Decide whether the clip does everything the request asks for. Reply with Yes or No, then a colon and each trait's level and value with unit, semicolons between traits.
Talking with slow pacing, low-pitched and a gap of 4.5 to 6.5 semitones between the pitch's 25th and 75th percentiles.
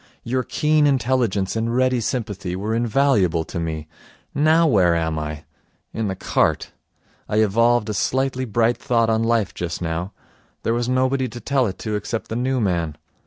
No: average, 170 wpm; low, 115 Hz; average, 5.1 semitones